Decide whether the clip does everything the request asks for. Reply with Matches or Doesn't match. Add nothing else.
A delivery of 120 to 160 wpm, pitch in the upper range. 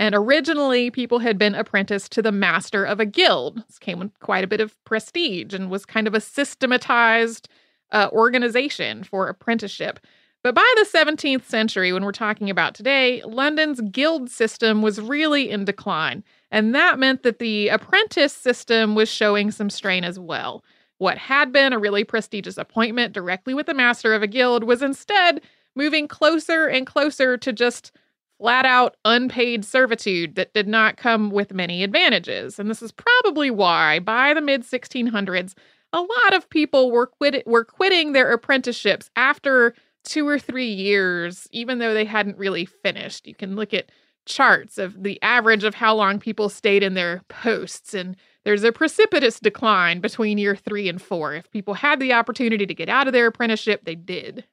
Doesn't match